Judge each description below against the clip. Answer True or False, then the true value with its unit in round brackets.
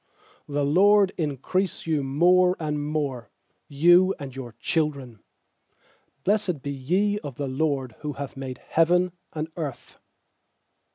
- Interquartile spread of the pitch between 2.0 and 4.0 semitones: False (4.7 semitones)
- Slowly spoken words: True (120 wpm)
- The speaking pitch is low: False (150 Hz)